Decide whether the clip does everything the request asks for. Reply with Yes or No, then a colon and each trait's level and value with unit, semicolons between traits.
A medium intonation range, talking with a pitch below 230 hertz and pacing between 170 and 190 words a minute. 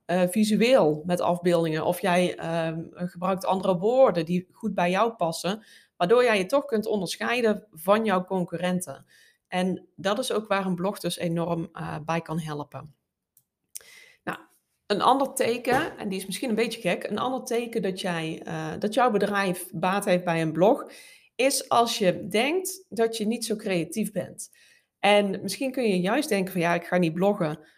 Yes: average, 4.3 semitones; high, 190 Hz; average, 180 wpm